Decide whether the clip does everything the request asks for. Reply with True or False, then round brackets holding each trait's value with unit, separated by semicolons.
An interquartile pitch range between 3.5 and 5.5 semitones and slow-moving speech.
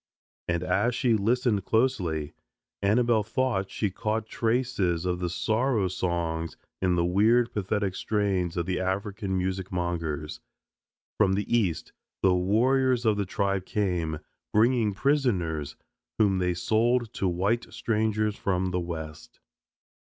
True (4.0 semitones; 130 wpm)